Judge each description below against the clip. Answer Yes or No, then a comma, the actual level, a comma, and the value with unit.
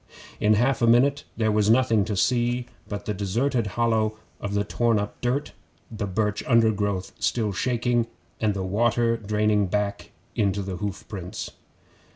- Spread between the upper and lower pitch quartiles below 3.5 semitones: Yes, narrow, 2.6 semitones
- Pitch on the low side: Yes, low, 110 Hz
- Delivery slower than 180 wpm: Yes, average, 160 wpm